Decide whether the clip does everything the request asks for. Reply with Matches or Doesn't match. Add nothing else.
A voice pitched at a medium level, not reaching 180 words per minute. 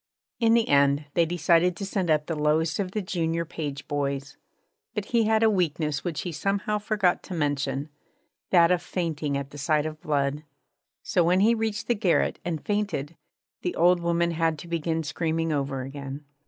Doesn't match